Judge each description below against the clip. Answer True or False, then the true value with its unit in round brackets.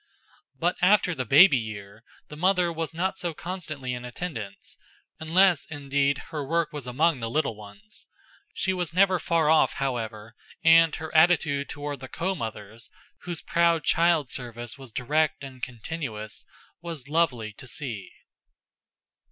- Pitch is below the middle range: False (150 Hz)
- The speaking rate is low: False (145 wpm)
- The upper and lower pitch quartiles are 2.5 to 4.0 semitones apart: False (5.4 semitones)